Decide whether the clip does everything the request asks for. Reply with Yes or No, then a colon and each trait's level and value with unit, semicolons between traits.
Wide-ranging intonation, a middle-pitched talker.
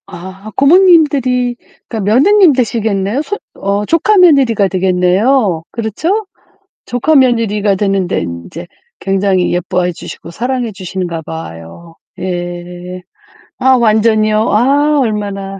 No: wide, 5.9 semitones; high, 210 Hz